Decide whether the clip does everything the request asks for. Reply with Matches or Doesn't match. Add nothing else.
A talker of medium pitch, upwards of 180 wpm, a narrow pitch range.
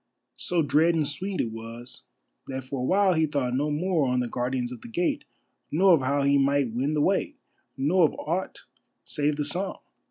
Doesn't match